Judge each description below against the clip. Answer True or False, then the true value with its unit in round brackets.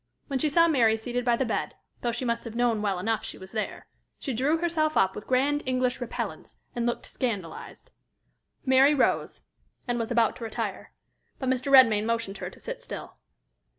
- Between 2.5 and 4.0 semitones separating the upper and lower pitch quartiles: True (2.9 semitones)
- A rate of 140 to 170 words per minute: False (190 wpm)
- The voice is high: True (240 Hz)